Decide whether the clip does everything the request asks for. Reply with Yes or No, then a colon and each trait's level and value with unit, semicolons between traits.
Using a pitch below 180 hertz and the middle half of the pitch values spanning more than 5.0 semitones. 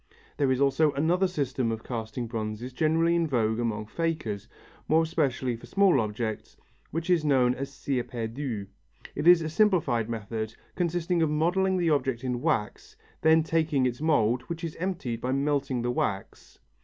Yes: low, 135 Hz; wide, 5.5 semitones